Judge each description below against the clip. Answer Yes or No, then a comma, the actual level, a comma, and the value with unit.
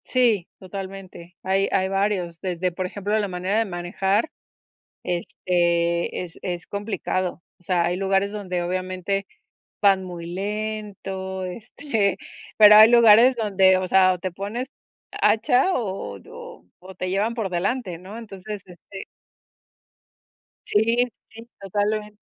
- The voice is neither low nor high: No, high, 195 Hz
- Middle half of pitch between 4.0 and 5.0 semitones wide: No, narrow, 2.6 semitones